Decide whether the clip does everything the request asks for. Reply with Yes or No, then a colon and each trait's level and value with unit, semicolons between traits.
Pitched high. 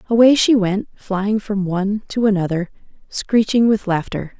Yes: high, 205 Hz